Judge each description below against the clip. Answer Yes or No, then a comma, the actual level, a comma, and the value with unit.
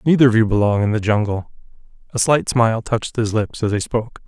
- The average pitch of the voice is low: Yes, low, 110 Hz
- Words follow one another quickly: Yes, fast, 225 wpm